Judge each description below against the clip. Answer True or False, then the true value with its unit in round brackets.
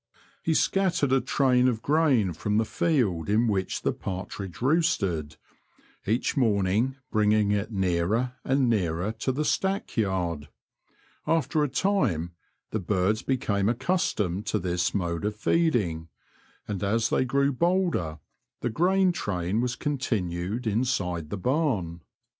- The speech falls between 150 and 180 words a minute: False (135 wpm)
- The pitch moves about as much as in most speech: False (6.4 semitones)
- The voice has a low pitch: True (110 Hz)